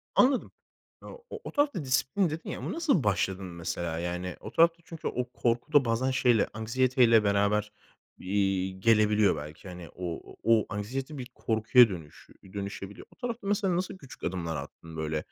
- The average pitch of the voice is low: Yes, low, 110 Hz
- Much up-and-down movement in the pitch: Yes, wide, 6.4 semitones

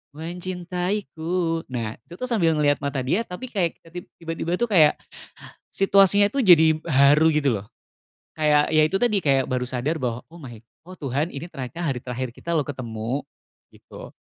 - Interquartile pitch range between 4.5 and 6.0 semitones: Yes, average, 5.0 semitones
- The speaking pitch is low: No, medium, 160 Hz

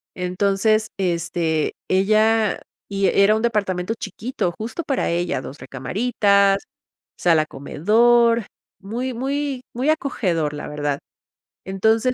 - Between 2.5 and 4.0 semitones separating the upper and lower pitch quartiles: No, average, 4.8 semitones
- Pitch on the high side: Yes, high, 200 Hz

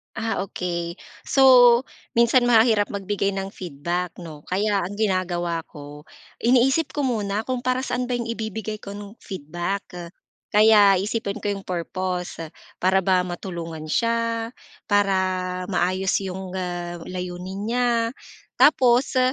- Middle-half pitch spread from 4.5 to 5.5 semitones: No, average, 3.9 semitones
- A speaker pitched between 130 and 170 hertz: No, high, 195 Hz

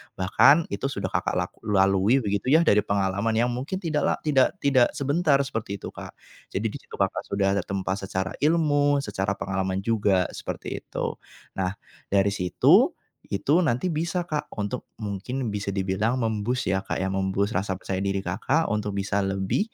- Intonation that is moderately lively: No, wide, 5.7 semitones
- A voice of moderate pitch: No, low, 105 Hz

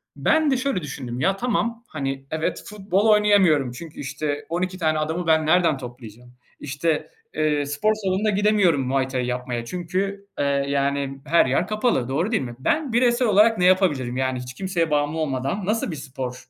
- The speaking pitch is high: No, medium, 160 Hz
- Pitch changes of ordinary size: No, wide, 6.7 semitones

